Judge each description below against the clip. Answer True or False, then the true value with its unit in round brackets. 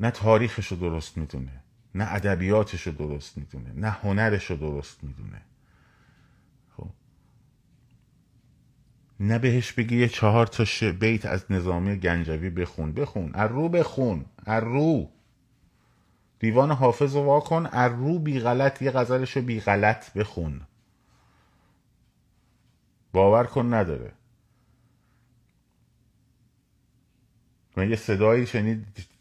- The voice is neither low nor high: False (110 Hz)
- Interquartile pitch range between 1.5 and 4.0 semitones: False (4.4 semitones)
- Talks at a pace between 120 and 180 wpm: False (110 wpm)